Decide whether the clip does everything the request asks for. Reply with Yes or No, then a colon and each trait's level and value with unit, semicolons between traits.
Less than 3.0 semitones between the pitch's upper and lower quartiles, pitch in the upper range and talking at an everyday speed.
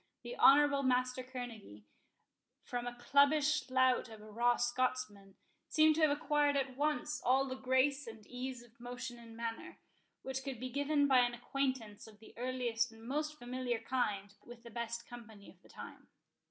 Yes: narrow, 2.6 semitones; very high, 250 Hz; average, 175 wpm